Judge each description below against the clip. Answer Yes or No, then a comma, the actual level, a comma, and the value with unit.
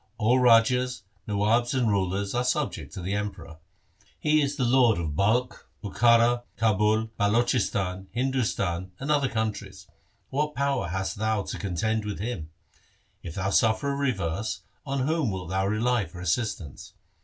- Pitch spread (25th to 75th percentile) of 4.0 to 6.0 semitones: Yes, average, 4.3 semitones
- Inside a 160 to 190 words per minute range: No, average, 150 wpm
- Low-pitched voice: Yes, low, 110 Hz